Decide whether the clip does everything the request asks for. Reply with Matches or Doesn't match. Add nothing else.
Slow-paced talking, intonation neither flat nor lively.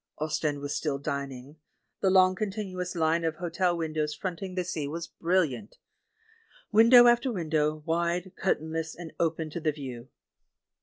Doesn't match